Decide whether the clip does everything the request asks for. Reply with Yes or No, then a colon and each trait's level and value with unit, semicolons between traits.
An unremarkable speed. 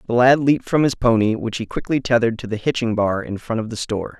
No: fast, 270 wpm